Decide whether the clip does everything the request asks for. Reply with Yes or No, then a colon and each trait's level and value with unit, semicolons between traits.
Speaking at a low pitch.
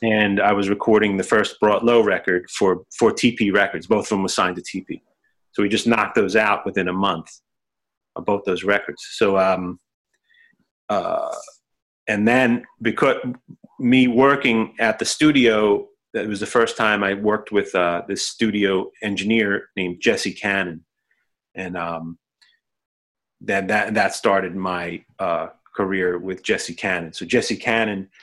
Yes: low, 105 Hz